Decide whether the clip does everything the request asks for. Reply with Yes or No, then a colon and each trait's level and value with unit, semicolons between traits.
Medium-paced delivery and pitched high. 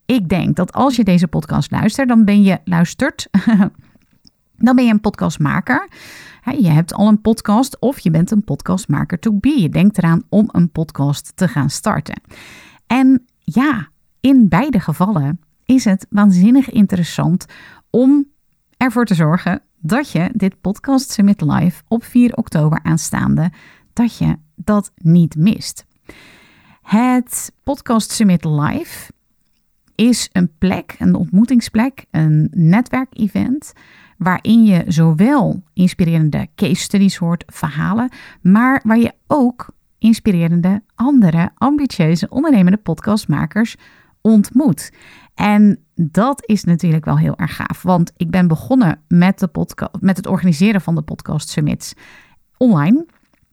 No: slow, 130 wpm; high, 200 Hz